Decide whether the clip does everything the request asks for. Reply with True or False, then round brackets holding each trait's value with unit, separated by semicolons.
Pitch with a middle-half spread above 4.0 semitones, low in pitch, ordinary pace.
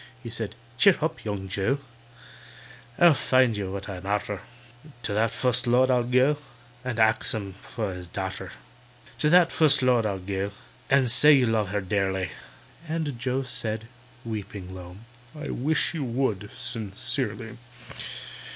True (4.5 semitones; 115 Hz; 150 wpm)